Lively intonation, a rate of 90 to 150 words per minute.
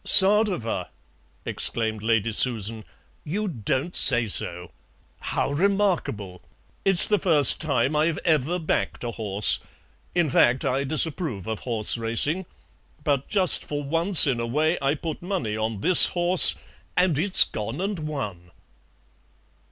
Yes: wide, 7.5 semitones; slow, 135 wpm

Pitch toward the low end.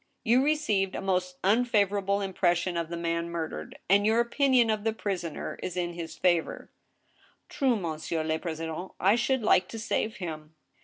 No: high, 190 Hz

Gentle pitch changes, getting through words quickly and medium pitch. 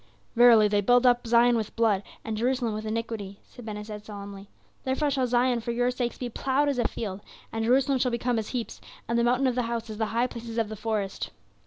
No: narrow, 2.3 semitones; fast, 230 wpm; high, 235 Hz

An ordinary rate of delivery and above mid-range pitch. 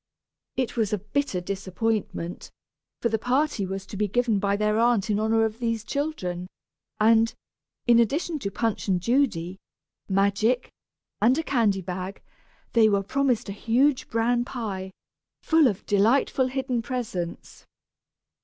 Yes: average, 145 wpm; high, 225 Hz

